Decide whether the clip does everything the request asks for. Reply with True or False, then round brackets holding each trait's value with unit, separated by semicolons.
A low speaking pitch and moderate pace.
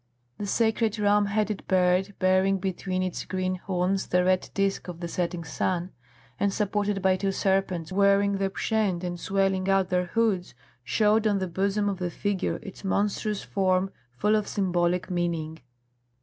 False (190 Hz; 165 wpm)